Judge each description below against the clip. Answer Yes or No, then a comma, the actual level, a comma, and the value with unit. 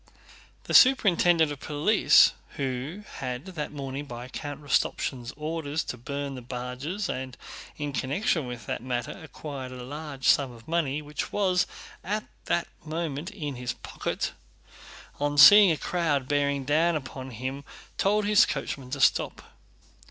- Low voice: No, medium, 145 Hz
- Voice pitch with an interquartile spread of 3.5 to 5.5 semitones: Yes, average, 4.2 semitones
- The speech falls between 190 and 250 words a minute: No, average, 150 wpm